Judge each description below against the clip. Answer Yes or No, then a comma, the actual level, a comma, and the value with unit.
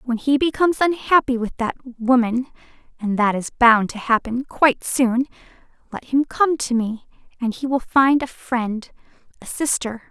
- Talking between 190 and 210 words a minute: No, average, 165 wpm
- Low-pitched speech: No, very high, 250 Hz